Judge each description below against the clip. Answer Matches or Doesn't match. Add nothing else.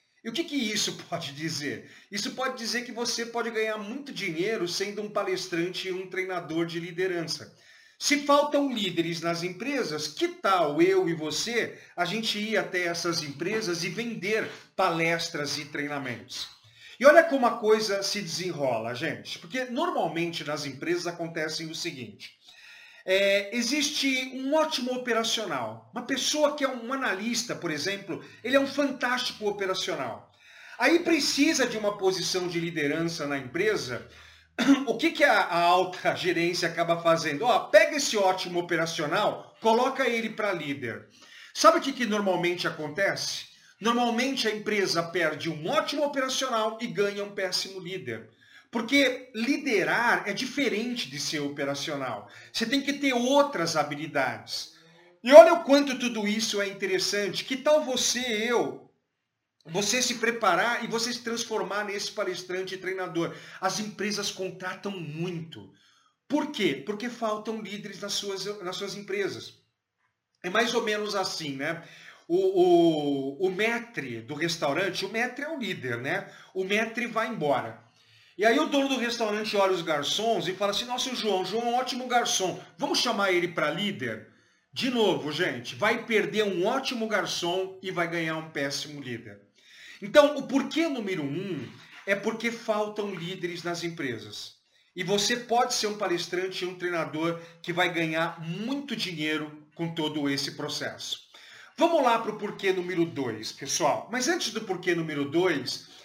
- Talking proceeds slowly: Doesn't match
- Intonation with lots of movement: Matches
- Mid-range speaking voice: Doesn't match